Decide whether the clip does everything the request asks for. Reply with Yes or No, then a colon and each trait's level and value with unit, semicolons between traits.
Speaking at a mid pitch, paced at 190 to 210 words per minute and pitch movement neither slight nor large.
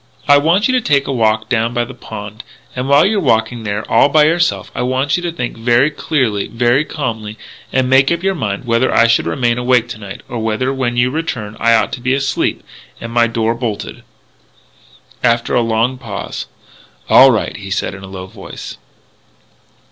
No: low, 120 Hz; average, 200 wpm; average, 3.4 semitones